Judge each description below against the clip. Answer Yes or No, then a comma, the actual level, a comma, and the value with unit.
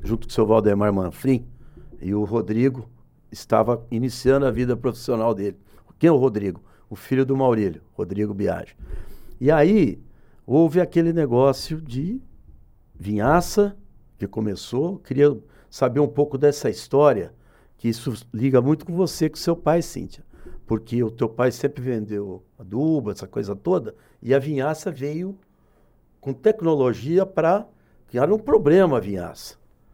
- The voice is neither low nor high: No, low, 130 Hz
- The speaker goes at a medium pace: Yes, average, 145 wpm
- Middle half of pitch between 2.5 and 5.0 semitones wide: No, wide, 5.5 semitones